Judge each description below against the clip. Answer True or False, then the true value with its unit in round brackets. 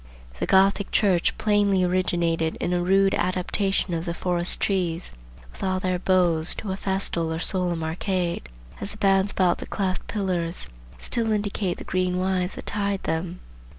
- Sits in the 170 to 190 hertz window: True (185 Hz)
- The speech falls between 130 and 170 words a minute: True (165 wpm)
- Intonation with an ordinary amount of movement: False (2.0 semitones)